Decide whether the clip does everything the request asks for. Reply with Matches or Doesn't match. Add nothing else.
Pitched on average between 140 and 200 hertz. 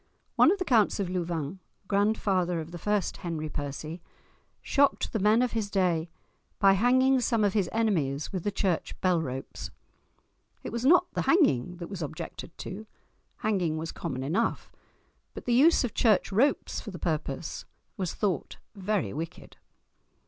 Matches